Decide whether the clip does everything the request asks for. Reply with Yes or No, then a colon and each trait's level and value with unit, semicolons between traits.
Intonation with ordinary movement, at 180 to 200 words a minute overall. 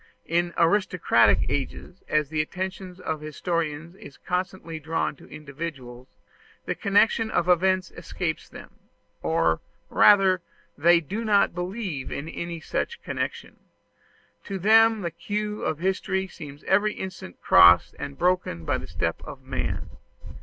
No: average, 3.9 semitones; slow, 135 wpm